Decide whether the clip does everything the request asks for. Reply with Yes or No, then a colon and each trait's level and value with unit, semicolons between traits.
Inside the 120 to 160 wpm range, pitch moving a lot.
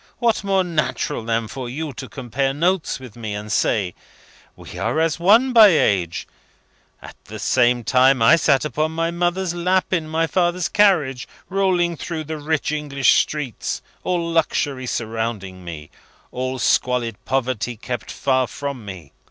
Yes: average, 155 wpm; wide, 6.0 semitones